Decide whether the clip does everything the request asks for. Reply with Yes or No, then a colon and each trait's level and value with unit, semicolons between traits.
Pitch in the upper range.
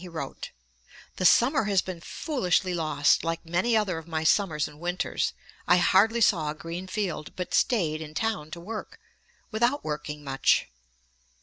No: medium, 175 Hz